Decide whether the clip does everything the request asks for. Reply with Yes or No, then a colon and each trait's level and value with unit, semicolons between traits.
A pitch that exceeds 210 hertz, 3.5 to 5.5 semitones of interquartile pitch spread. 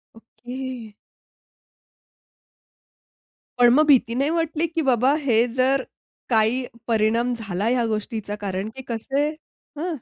Yes: high, 245 Hz; average, 3.8 semitones